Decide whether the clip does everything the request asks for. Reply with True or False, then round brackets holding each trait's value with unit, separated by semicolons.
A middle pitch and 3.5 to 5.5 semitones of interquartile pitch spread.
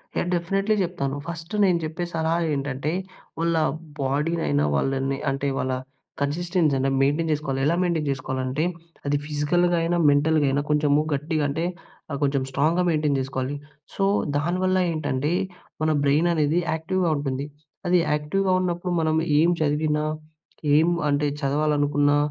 False (150 Hz; 3.1 semitones)